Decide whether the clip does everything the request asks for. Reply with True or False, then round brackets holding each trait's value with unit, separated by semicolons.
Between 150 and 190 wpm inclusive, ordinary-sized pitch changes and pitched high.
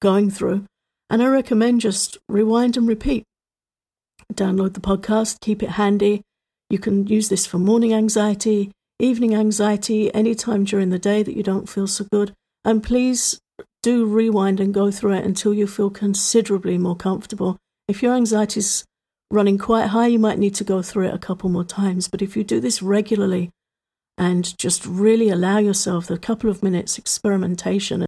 False (175 wpm; 2.0 semitones; 205 Hz)